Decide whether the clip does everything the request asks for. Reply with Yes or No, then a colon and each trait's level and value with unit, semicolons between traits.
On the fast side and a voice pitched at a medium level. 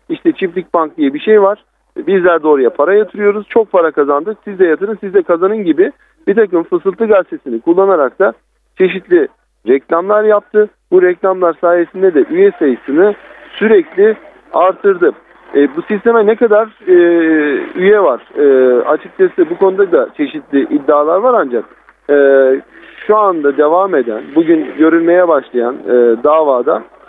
No: fast, 145 wpm; high, 205 Hz